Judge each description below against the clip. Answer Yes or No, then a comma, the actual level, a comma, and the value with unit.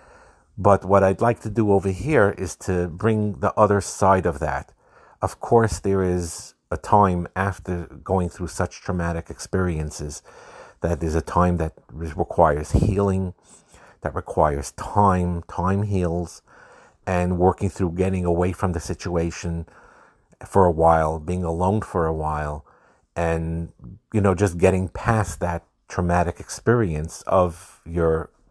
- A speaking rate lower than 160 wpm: Yes, average, 140 wpm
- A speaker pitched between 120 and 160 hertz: No, very low, 90 Hz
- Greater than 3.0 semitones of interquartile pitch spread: No, narrow, 2.6 semitones